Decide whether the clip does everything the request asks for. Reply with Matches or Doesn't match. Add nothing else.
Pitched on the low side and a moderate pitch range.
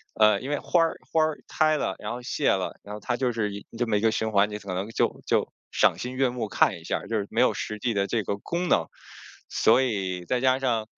Matches